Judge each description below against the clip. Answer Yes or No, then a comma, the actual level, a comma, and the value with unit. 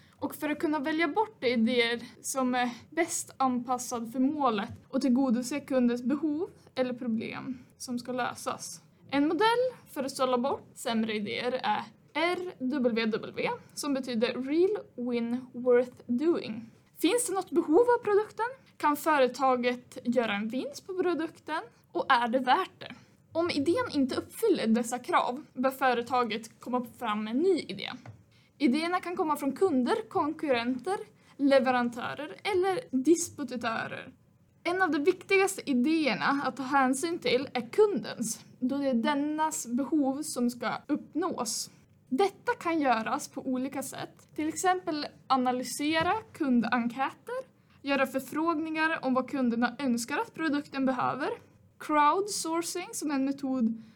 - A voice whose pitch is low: No, very high, 270 Hz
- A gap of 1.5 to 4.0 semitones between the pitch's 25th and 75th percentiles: No, average, 5.1 semitones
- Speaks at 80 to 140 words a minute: Yes, average, 135 wpm